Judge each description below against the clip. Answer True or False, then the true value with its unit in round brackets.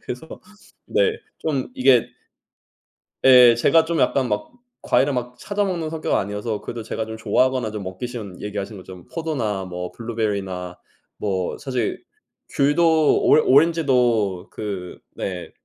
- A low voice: True (120 Hz)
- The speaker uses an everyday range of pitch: False (5.7 semitones)